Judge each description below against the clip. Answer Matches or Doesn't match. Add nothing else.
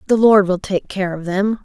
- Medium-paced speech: Doesn't match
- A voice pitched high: Matches